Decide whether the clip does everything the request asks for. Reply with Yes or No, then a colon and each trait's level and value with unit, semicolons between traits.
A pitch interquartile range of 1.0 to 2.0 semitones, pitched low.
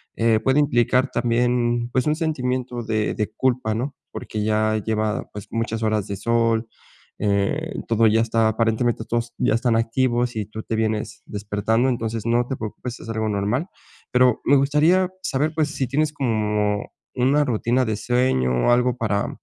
No: average, 2.7 semitones; low, 115 Hz